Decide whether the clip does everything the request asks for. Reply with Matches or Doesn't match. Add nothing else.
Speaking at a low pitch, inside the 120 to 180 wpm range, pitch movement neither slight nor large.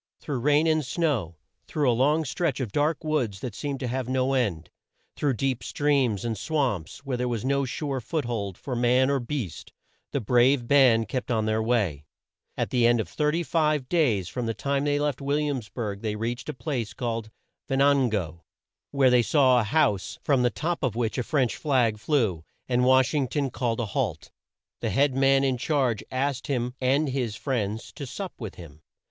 Doesn't match